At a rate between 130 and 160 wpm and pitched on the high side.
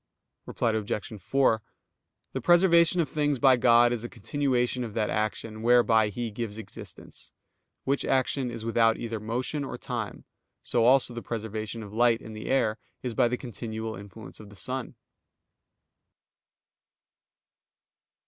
No: average, 145 wpm; low, 115 Hz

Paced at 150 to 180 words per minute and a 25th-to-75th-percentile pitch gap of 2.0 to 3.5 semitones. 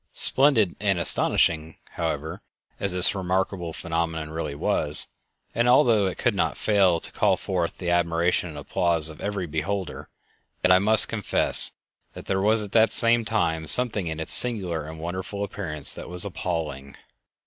No: average, 160 wpm; average, 4.0 semitones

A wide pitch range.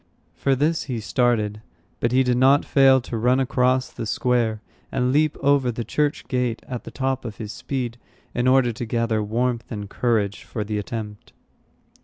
No: average, 2.8 semitones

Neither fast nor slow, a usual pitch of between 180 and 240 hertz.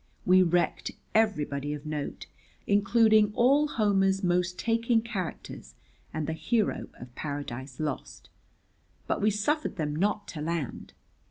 No: slow, 125 wpm; medium, 185 Hz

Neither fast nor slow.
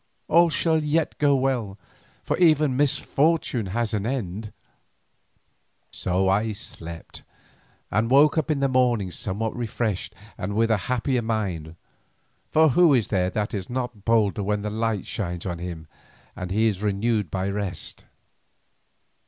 Yes: average, 145 wpm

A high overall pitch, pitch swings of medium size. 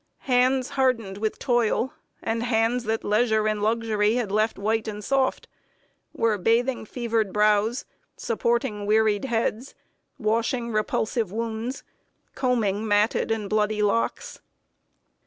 No: high, 225 Hz; narrow, 2.1 semitones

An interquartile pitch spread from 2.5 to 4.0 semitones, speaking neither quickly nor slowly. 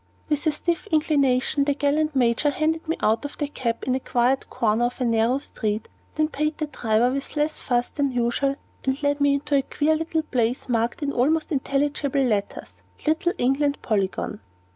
Yes: average, 3.7 semitones; average, 185 wpm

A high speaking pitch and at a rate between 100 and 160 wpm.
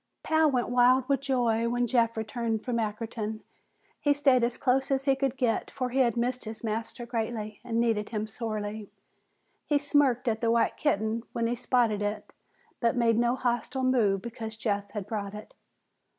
No: high, 235 Hz; average, 180 wpm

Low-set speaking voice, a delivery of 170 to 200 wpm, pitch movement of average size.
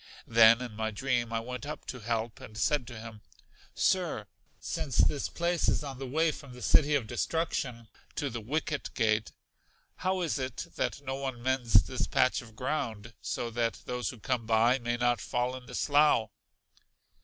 Yes: low, 125 Hz; average, 185 wpm; average, 3.3 semitones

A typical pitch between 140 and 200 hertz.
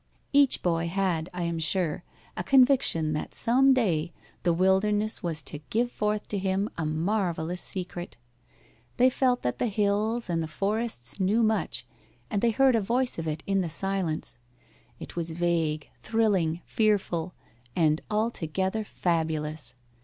Yes: medium, 185 Hz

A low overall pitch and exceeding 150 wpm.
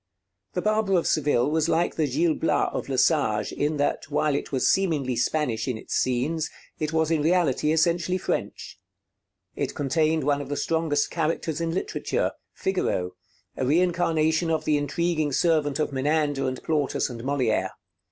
No: medium, 155 Hz; average, 160 wpm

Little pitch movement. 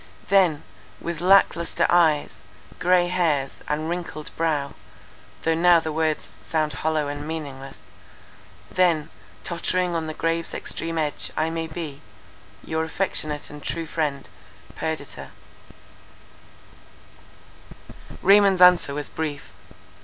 Yes: narrow, 2.2 semitones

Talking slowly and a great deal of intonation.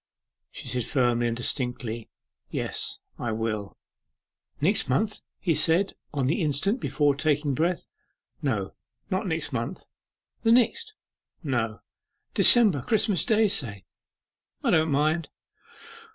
Yes: slow, 120 wpm; wide, 7.4 semitones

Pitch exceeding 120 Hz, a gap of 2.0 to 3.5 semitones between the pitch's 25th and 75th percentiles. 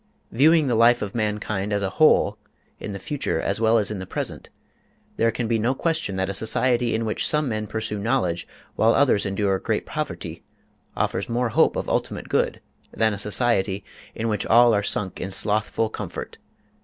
No: low, 110 Hz; average, 2.8 semitones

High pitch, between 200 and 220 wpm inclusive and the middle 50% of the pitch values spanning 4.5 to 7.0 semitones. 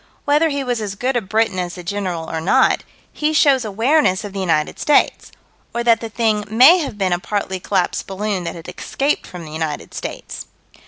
Yes: high, 210 Hz; fast, 205 wpm; average, 5.3 semitones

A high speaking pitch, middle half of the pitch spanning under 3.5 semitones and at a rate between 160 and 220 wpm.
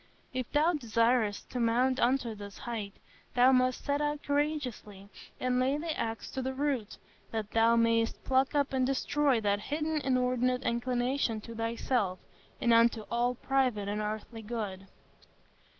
No: high, 245 Hz; average, 2.9 semitones; average, 150 wpm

